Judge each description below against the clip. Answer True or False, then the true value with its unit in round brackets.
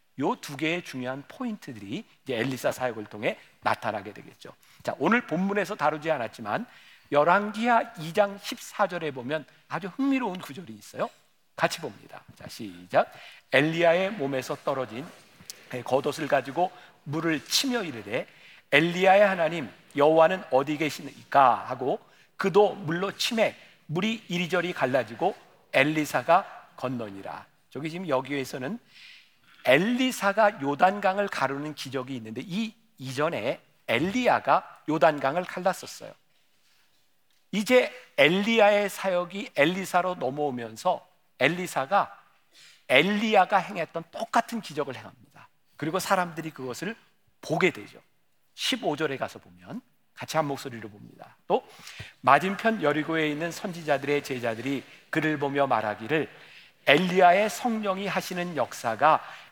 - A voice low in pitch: False (160 Hz)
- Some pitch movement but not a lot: False (5.9 semitones)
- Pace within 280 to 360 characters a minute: True (290 characters per minute)